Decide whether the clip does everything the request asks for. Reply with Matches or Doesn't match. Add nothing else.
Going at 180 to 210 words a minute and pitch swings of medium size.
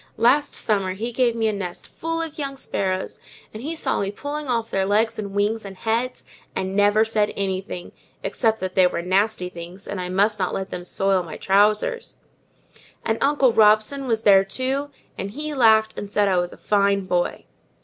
Matches